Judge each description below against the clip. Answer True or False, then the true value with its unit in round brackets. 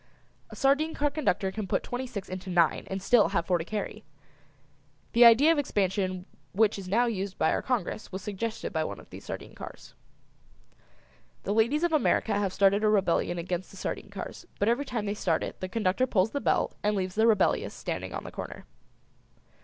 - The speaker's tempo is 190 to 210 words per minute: True (200 wpm)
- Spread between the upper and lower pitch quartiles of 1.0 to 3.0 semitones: False (4.0 semitones)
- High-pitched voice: True (205 Hz)